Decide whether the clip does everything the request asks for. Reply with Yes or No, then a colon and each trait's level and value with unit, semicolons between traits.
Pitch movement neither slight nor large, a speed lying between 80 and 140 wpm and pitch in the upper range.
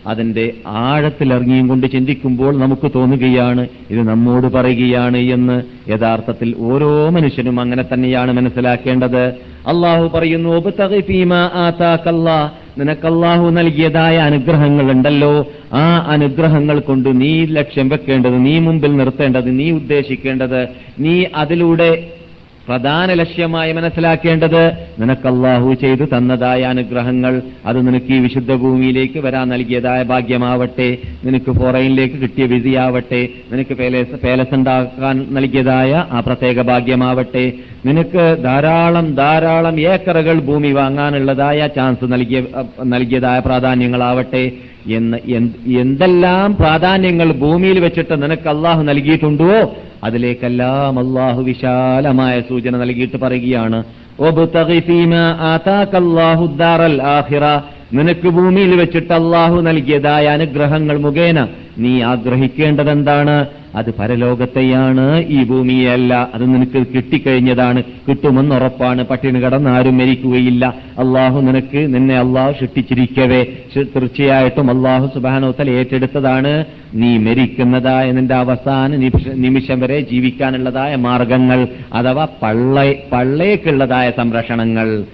No: average, 3.1 semitones; average, 90 wpm; low, 130 Hz